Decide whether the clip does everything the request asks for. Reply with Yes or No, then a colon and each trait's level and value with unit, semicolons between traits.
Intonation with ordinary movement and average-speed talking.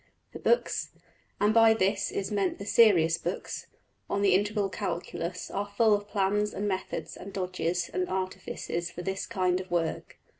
No: narrow, 2.2 semitones; average, 165 wpm